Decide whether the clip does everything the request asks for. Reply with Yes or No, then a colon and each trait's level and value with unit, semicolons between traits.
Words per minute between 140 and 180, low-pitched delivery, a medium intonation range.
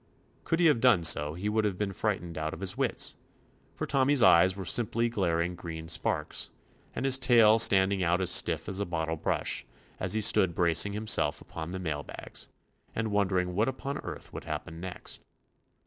No: average, 195 wpm; very low, 95 Hz; average, 4.4 semitones